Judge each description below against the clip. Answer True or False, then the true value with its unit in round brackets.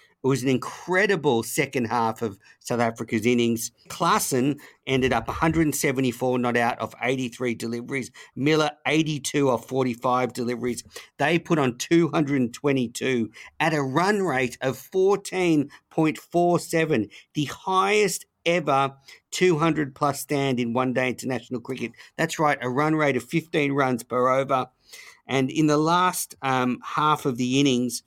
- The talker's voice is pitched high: False (135 Hz)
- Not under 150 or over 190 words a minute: False (135 wpm)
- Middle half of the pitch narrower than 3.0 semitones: False (3.9 semitones)